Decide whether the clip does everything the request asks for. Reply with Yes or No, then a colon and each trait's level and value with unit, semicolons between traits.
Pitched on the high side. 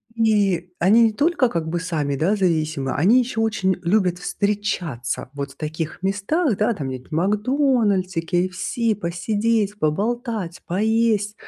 Yes: high, 195 Hz